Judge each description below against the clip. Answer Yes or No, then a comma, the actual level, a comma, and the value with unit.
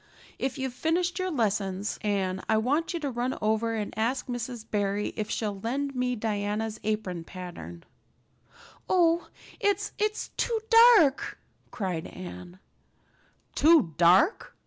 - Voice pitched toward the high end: Yes, high, 225 Hz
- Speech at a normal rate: No, slow, 130 wpm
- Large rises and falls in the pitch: Yes, wide, 6.1 semitones